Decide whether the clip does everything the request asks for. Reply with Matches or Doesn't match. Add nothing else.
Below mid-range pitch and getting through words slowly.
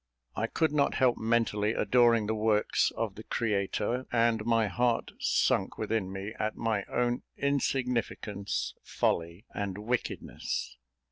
Matches